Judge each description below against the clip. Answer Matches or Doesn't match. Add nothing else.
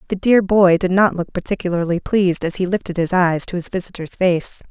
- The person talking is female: Matches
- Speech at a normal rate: Doesn't match